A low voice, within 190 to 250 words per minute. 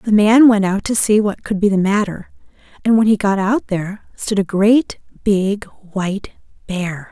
No: high, 200 Hz; average, 195 wpm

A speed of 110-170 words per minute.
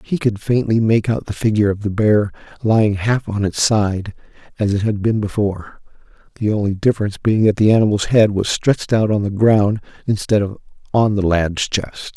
No: average, 195 wpm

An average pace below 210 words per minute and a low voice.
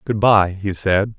Yes: average, 200 wpm; low, 100 Hz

